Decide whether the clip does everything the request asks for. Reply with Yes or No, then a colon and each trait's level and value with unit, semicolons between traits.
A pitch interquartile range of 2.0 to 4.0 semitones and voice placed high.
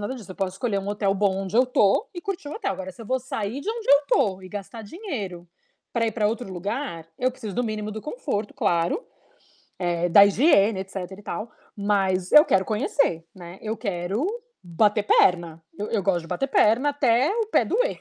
No: average, 5.3 semitones; high, 210 Hz